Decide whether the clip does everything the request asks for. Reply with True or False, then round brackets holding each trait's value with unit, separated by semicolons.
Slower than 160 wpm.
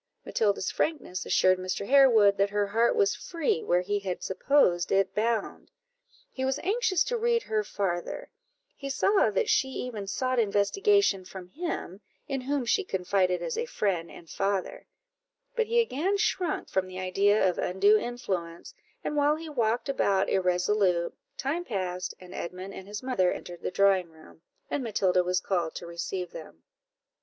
False (165 wpm)